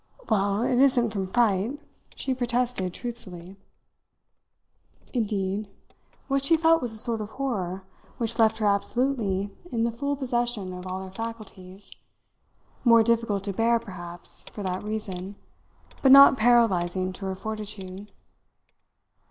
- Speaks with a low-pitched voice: No, high, 215 Hz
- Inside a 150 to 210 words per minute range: No, slow, 135 wpm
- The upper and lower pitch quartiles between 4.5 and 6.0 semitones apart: No, average, 4.0 semitones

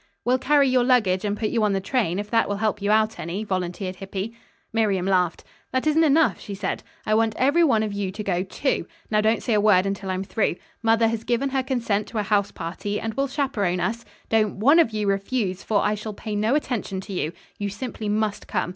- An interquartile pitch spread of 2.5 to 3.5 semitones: Yes, average, 3.1 semitones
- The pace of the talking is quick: Yes, fast, 235 wpm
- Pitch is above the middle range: Yes, high, 215 Hz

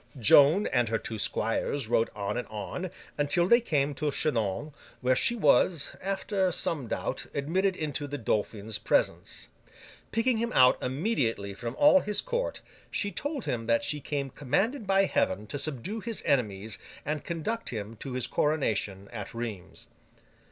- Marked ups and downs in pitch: Yes, wide, 8.9 semitones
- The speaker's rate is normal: Yes, average, 160 wpm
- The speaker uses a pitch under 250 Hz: Yes, medium, 140 Hz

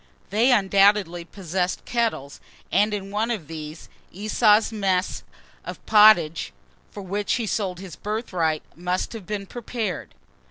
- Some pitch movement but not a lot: Yes, average, 3.3 semitones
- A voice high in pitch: Yes, high, 200 Hz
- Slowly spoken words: Yes, slow, 130 wpm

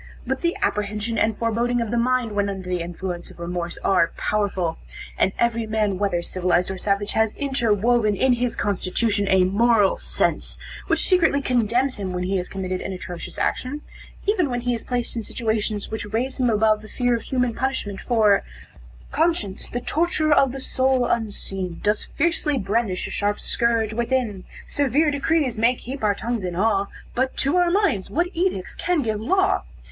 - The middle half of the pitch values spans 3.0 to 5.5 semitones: Yes, average, 4.3 semitones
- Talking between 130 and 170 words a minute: No, average, 180 wpm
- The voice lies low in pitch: No, high, 225 Hz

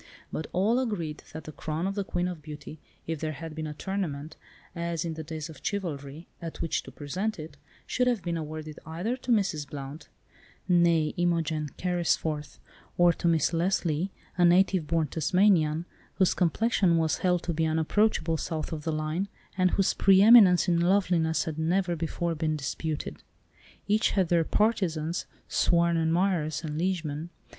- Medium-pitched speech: Yes, medium, 165 Hz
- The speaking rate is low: No, average, 165 wpm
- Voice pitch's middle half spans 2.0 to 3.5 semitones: Yes, average, 2.9 semitones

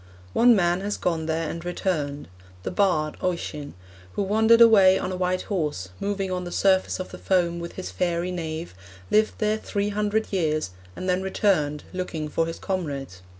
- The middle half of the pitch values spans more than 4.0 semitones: No, average, 3.6 semitones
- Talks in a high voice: No, medium, 180 Hz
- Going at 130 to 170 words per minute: No, average, 180 wpm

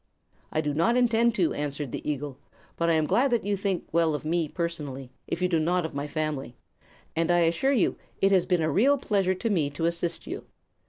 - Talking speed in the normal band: No, fast, 225 wpm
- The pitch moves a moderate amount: Yes, average, 4.4 semitones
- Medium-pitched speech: Yes, medium, 170 Hz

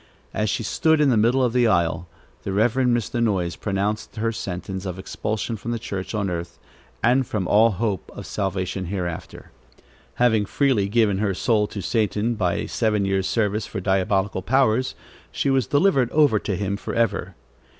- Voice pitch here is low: Yes, low, 105 Hz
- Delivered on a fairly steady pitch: No, average, 3.5 semitones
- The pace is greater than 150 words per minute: Yes, average, 175 wpm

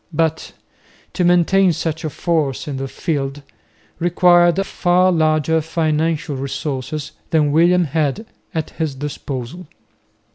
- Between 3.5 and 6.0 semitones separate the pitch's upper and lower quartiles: No, average, 3.0 semitones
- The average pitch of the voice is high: No, medium, 160 Hz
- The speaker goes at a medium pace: No, slow, 115 wpm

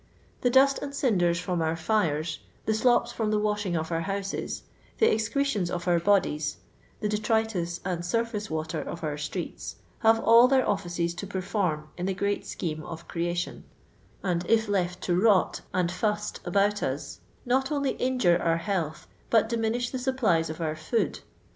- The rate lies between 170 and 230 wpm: Yes, average, 175 wpm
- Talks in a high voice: Yes, high, 195 Hz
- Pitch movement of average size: Yes, average, 4.7 semitones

